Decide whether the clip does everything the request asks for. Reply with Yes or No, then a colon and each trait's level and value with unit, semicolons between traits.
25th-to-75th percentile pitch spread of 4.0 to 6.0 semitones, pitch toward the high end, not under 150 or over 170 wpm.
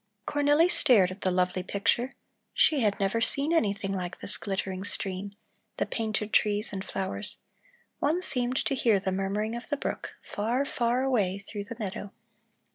Yes: average, 4.3 semitones; high, 210 Hz; average, 165 wpm